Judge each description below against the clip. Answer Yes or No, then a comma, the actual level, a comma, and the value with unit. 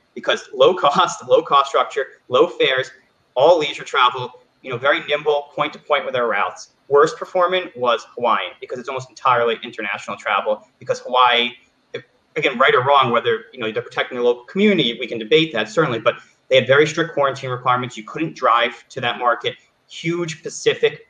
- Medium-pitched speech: Yes, medium, 175 Hz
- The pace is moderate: Yes, average, 185 wpm